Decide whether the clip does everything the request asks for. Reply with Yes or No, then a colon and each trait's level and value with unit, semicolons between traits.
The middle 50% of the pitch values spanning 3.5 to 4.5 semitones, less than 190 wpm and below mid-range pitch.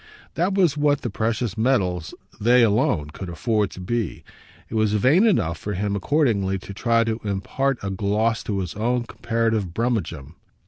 Yes: average, 3.9 semitones; average, 170 wpm; low, 110 Hz